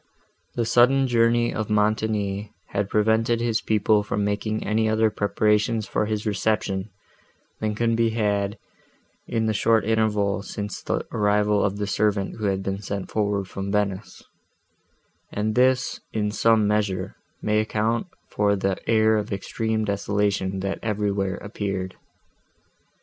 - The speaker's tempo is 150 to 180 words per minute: No, average, 140 wpm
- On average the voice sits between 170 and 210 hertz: No, low, 105 Hz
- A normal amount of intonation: No, narrow, 1.5 semitones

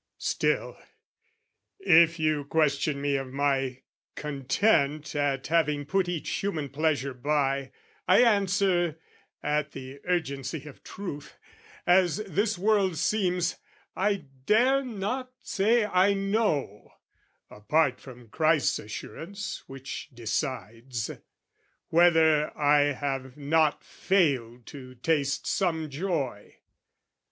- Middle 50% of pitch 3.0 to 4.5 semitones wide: No, average, 5.0 semitones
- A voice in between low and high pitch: Yes, medium, 155 Hz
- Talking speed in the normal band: No, slow, 105 wpm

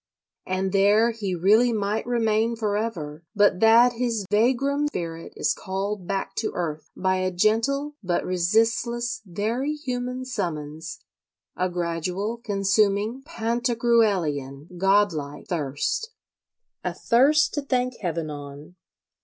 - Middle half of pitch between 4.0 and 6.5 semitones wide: Yes, average, 4.9 semitones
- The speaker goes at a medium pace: No, slow, 120 wpm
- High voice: Yes, high, 205 Hz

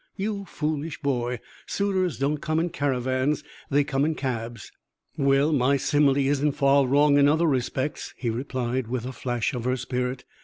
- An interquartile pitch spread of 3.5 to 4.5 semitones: No, average, 2.8 semitones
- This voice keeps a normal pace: Yes, average, 165 wpm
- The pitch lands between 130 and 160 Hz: Yes, medium, 140 Hz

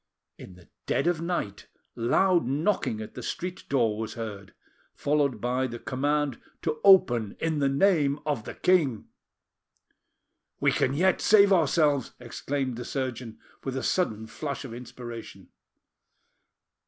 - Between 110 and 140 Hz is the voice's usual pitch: Yes, low, 135 Hz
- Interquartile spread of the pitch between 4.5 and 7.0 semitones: Yes, average, 5.0 semitones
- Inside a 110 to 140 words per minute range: Yes, slow, 135 wpm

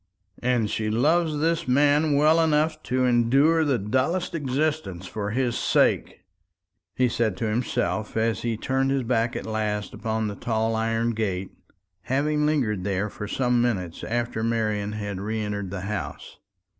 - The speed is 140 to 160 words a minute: Yes, average, 155 wpm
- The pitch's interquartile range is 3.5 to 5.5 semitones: Yes, average, 4.5 semitones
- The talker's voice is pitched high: No, low, 115 Hz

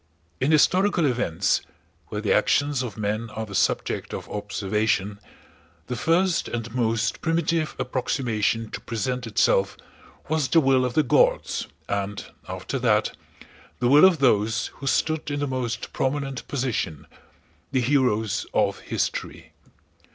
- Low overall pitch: Yes, low, 125 Hz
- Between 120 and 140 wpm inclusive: Yes, slow, 135 wpm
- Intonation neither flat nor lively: Yes, average, 4.9 semitones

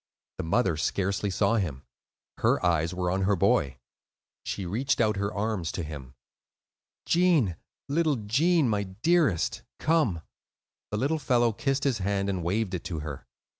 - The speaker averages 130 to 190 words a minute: Yes, average, 155 wpm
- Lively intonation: Yes, wide, 6.5 semitones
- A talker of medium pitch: No, low, 100 Hz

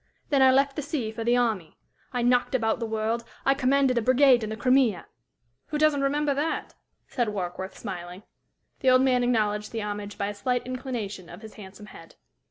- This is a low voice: No, high, 235 Hz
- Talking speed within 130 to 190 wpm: No, average, 200 wpm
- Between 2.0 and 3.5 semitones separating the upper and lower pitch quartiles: No, average, 4.1 semitones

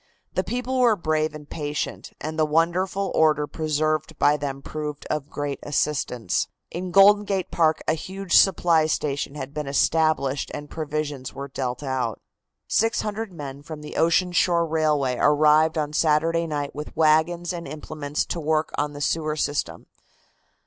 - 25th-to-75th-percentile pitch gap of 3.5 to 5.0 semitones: No, narrow, 2.4 semitones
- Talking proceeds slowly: No, average, 160 wpm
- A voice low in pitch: No, medium, 155 Hz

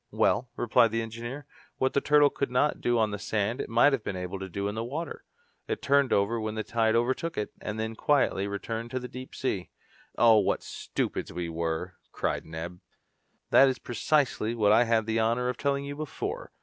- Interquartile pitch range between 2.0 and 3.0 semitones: No, average, 3.9 semitones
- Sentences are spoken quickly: Yes, fast, 210 wpm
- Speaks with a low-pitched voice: Yes, low, 115 Hz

